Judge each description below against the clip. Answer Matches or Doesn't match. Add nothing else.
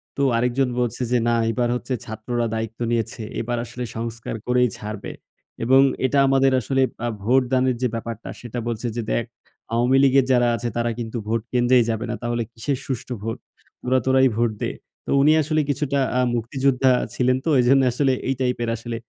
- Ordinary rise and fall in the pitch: Doesn't match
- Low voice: Matches